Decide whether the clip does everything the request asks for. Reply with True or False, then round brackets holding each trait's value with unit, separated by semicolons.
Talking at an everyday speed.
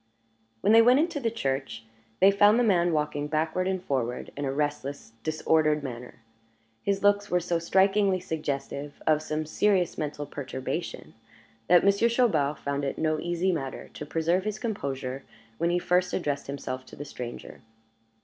True (165 wpm)